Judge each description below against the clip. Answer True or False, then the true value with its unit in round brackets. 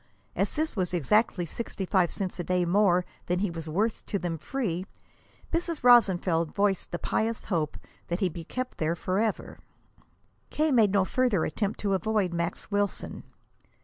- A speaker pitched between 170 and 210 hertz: True (190 Hz)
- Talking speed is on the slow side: False (165 wpm)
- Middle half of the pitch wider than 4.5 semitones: False (4.0 semitones)